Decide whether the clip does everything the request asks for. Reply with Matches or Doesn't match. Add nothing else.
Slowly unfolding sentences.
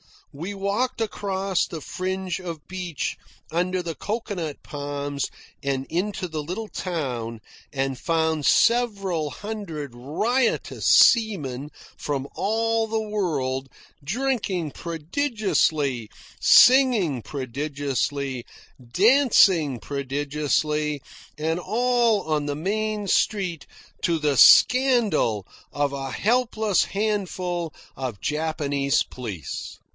Matches